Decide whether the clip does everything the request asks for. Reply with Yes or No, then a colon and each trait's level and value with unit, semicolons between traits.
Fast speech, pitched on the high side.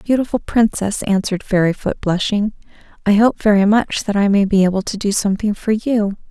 No: average, 180 wpm; high, 205 Hz